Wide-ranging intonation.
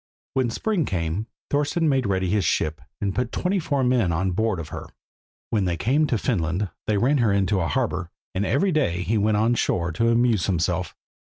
Yes: wide, 5.7 semitones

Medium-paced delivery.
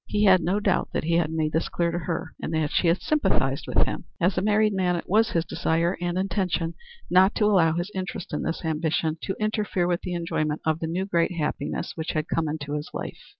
No: fast, 235 wpm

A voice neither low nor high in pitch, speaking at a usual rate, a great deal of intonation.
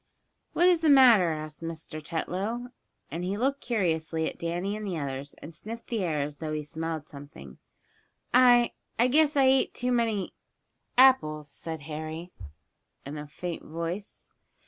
Yes: medium, 170 Hz; average, 160 wpm; wide, 7.5 semitones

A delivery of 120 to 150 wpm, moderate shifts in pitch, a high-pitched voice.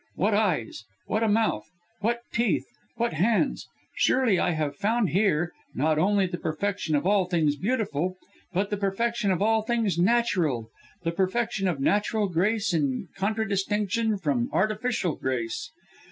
Yes: average, 145 wpm; average, 4.7 semitones; high, 195 Hz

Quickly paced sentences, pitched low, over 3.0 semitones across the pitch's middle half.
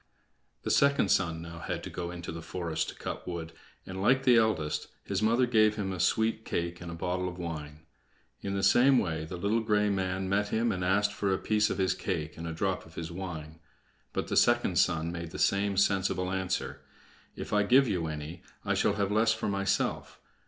Yes: fast, 215 wpm; very low, 95 Hz; average, 3.6 semitones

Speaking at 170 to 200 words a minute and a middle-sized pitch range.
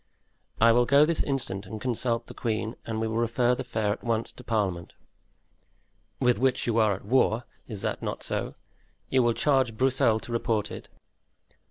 No: average, 180 wpm; narrow, 2.3 semitones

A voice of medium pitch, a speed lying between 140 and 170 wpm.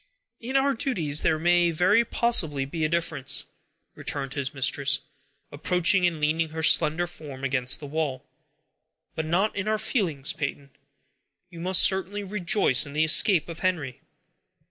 Yes: medium, 165 Hz; average, 150 wpm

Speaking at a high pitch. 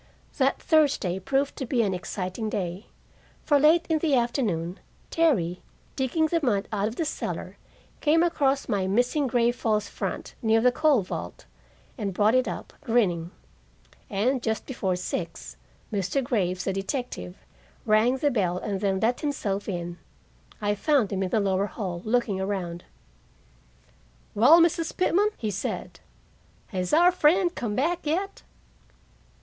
Yes: high, 225 Hz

